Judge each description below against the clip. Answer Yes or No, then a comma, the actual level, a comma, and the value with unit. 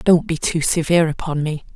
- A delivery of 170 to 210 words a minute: Yes, fast, 205 wpm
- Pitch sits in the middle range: Yes, medium, 160 Hz